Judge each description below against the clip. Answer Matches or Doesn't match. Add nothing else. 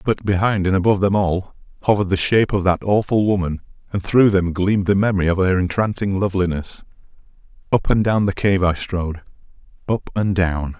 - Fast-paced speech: Doesn't match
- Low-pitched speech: Matches